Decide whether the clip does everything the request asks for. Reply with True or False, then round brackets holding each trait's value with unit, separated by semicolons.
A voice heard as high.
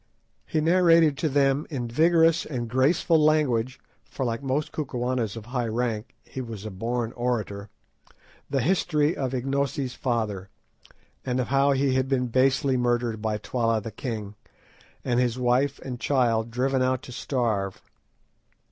False (125 Hz)